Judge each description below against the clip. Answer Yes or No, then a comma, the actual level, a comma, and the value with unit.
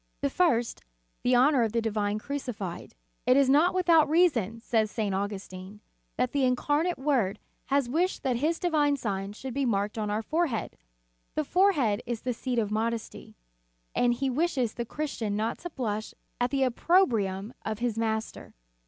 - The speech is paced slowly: No, average, 170 wpm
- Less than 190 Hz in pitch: No, high, 245 Hz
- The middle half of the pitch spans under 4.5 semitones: No, average, 4.9 semitones